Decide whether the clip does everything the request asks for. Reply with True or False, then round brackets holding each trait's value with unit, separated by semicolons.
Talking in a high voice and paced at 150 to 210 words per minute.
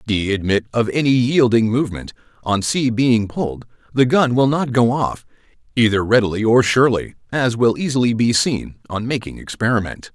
False (120 Hz; 170 wpm)